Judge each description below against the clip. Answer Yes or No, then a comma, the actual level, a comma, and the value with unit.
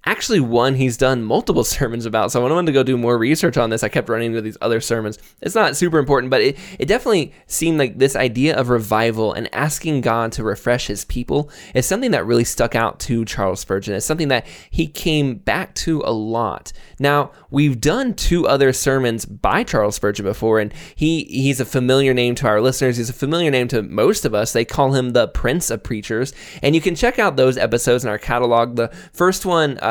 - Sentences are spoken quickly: Yes, fast, 225 wpm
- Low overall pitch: Yes, low, 130 Hz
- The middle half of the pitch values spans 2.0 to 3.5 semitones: No, average, 4.1 semitones